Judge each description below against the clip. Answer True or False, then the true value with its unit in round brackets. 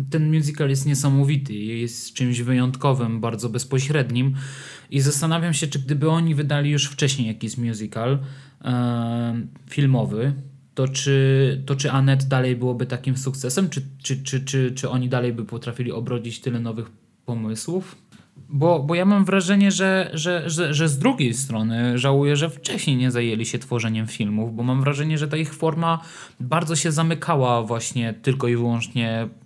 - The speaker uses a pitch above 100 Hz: True (135 Hz)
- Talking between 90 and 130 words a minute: False (160 wpm)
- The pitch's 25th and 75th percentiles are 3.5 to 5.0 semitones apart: True (3.8 semitones)